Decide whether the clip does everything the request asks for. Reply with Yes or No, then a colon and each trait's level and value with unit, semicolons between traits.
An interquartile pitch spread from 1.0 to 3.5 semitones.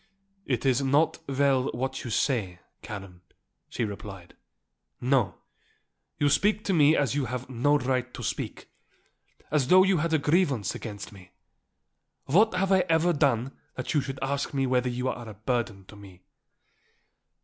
No: average, 4.2 semitones